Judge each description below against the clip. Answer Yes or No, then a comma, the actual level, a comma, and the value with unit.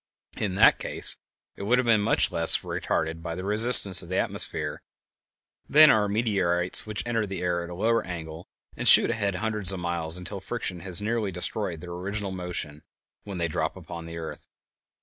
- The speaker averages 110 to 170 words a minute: No, average, 185 wpm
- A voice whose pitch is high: No, very low, 95 Hz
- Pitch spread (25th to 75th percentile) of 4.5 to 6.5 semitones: No, average, 3.5 semitones